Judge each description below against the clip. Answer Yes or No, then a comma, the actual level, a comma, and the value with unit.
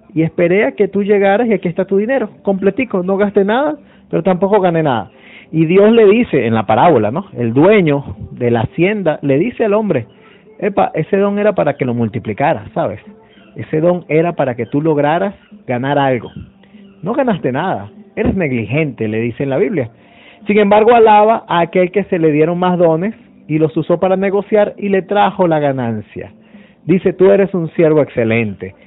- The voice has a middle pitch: Yes, medium, 180 Hz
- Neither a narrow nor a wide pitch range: No, wide, 6.1 semitones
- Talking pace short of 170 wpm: No, average, 190 wpm